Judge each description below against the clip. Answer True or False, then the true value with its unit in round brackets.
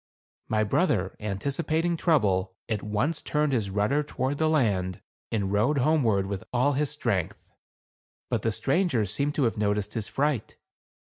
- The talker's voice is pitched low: True (115 Hz)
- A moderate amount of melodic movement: False (6.2 semitones)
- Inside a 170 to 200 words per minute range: False (145 wpm)